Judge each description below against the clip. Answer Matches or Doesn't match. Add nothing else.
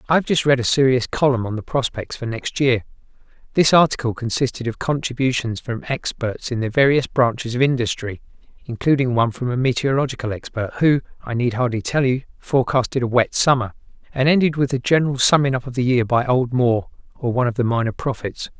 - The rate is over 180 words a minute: Matches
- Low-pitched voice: Matches